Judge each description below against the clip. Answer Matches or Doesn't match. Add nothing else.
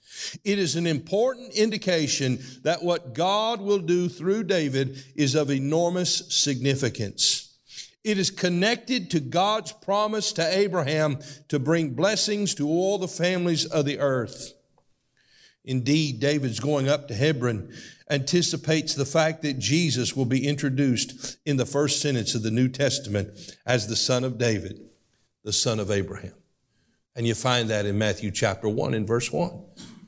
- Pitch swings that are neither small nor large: Doesn't match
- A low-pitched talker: Doesn't match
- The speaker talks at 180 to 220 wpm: Doesn't match